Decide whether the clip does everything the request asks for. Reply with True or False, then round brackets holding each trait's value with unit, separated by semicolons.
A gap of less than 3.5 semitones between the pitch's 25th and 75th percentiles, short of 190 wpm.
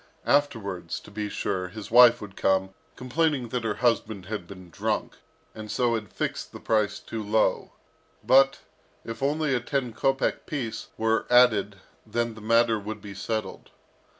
True (3.1 semitones; 160 wpm)